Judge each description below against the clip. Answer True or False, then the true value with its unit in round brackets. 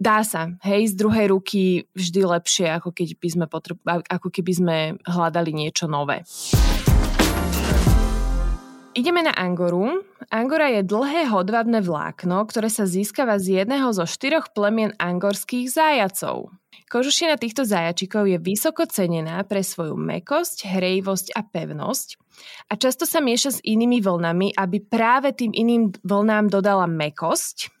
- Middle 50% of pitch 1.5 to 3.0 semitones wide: False (4.8 semitones)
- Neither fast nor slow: True (135 wpm)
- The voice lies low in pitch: False (195 Hz)